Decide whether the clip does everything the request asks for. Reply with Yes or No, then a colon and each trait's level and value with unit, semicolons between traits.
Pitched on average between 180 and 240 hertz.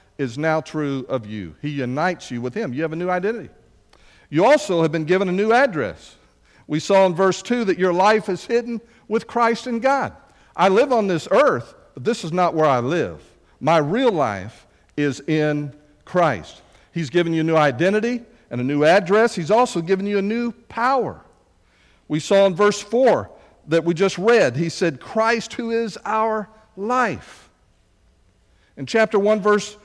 Yes: medium, 185 Hz